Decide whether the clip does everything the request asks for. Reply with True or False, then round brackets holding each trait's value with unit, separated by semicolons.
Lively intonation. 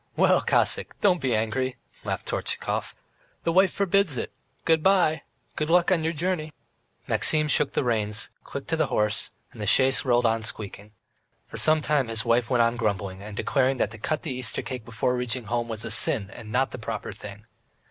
True (5.8 semitones)